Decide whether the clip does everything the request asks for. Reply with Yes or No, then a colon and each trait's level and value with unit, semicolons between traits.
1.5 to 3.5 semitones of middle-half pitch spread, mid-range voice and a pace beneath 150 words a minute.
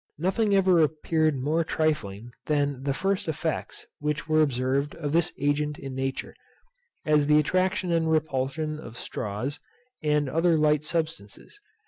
Yes: narrow, 2.6 semitones; medium, 150 Hz; average, 140 wpm